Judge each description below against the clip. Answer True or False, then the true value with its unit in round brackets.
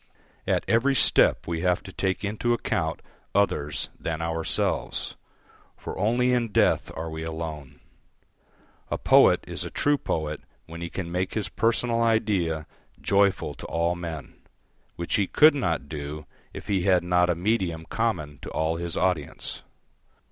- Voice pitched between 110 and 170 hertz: False (90 Hz)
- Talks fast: False (155 wpm)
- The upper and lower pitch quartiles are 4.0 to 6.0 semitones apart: True (4.6 semitones)